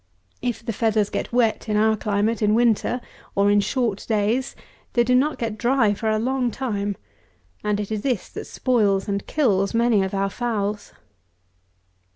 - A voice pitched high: Yes, high, 220 Hz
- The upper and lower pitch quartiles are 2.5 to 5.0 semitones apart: Yes, average, 2.9 semitones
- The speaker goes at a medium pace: Yes, average, 175 wpm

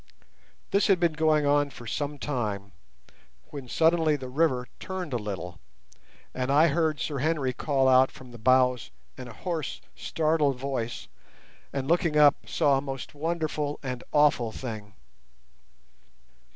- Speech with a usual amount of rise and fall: Yes, average, 3.6 semitones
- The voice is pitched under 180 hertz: Yes, medium, 140 Hz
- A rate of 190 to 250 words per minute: No, average, 145 wpm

